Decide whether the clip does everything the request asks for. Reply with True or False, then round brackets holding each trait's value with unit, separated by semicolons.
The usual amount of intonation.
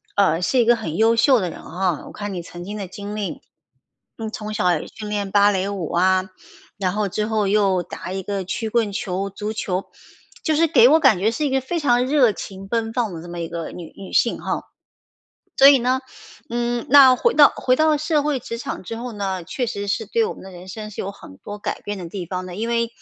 True (4.2 semitones)